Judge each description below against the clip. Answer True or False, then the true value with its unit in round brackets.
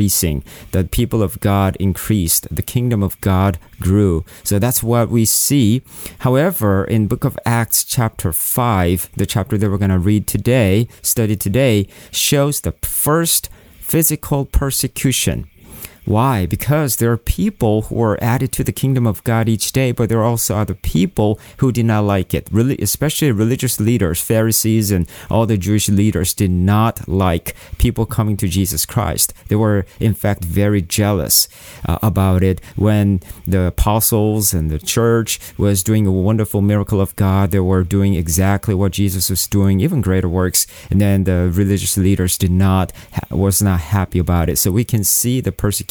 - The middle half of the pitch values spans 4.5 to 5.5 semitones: False (3.4 semitones)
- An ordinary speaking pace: True (175 wpm)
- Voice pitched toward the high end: False (100 Hz)